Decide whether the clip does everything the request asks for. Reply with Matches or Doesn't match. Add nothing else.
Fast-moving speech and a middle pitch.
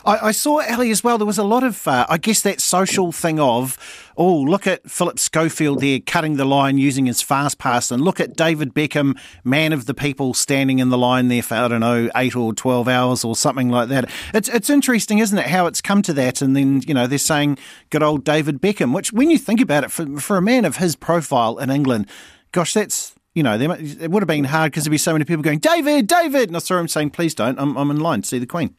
Matches